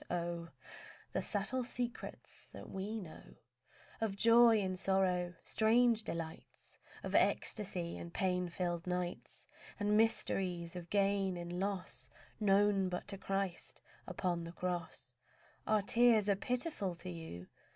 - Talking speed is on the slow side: Yes, slow, 130 wpm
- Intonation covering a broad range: No, average, 3.1 semitones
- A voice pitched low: No, high, 190 Hz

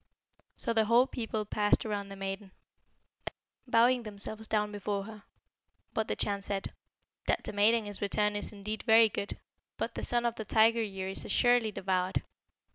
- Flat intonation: Yes, narrow, 2.0 semitones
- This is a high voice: Yes, high, 210 Hz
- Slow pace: No, average, 170 wpm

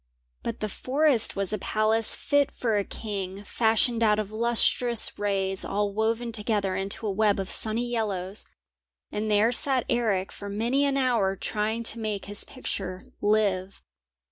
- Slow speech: No, average, 160 wpm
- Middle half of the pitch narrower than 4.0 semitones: Yes, average, 2.7 semitones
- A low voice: No, high, 215 Hz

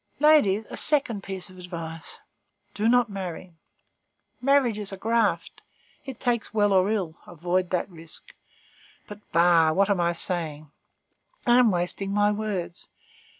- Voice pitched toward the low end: No, high, 195 Hz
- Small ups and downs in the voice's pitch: No, average, 3.9 semitones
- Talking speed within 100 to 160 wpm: Yes, average, 145 wpm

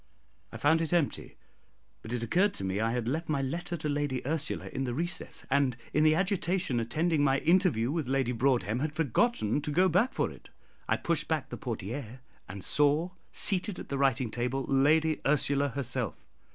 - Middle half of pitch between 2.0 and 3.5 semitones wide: No, average, 4.6 semitones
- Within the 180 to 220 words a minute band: Yes, average, 190 wpm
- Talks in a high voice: No, medium, 140 Hz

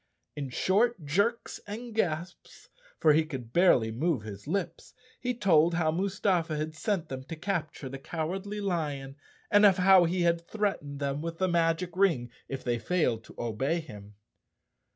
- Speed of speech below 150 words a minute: No, average, 165 wpm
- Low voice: No, medium, 165 Hz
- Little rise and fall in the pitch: No, average, 5.2 semitones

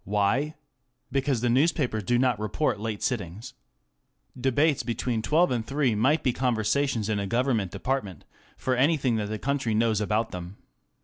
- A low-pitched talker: Yes, low, 120 Hz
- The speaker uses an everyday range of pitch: Yes, average, 4.0 semitones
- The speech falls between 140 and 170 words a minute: Yes, average, 160 wpm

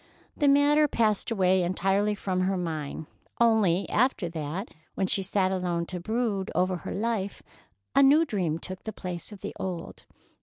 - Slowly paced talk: No, average, 160 wpm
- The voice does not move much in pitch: No, average, 3.6 semitones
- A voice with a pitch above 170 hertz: Yes, high, 190 Hz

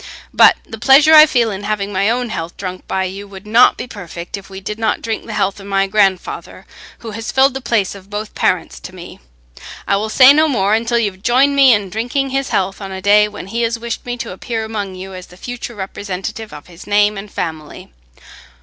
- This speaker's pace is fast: Yes, fast, 230 wpm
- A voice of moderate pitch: No, high, 210 Hz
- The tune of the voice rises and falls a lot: No, average, 3.4 semitones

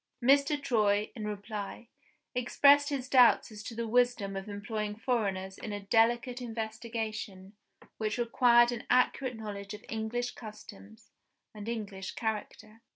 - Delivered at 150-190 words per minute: No, slow, 135 wpm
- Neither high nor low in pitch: No, high, 220 Hz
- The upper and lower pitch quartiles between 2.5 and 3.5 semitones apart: Yes, average, 2.8 semitones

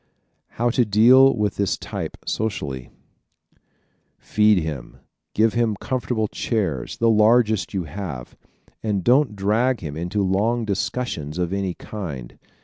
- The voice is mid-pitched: No, low, 105 Hz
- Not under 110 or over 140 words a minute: Yes, slow, 135 wpm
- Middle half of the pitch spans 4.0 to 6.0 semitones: Yes, average, 4.4 semitones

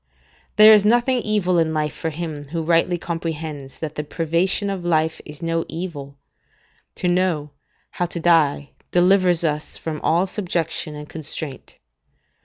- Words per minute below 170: Yes, average, 150 wpm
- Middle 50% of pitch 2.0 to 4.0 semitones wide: Yes, average, 2.7 semitones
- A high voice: No, medium, 165 Hz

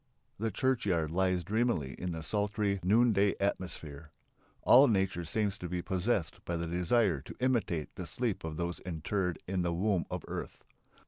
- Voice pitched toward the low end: Yes, very low, 95 Hz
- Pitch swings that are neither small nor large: Yes, average, 3.6 semitones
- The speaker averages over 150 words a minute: Yes, average, 165 wpm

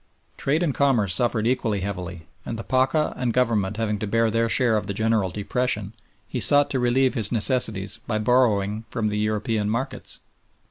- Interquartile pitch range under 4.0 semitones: Yes, average, 3.3 semitones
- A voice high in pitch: No, low, 110 Hz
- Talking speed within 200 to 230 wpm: No, average, 180 wpm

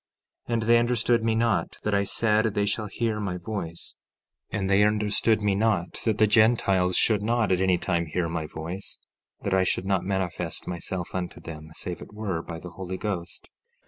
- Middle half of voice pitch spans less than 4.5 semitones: Yes, average, 3.3 semitones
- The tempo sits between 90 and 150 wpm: No, average, 190 wpm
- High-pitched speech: No, low, 100 Hz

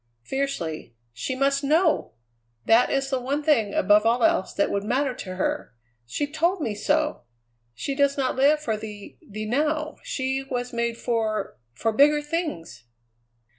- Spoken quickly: No, average, 160 wpm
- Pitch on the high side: Yes, very high, 260 Hz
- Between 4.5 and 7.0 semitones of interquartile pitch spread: Yes, average, 5.2 semitones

